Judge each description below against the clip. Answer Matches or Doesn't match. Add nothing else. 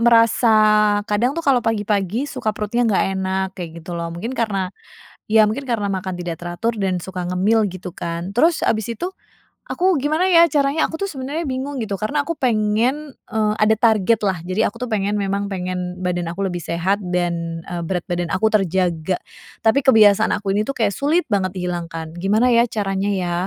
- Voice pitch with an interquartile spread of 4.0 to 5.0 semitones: Matches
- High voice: Matches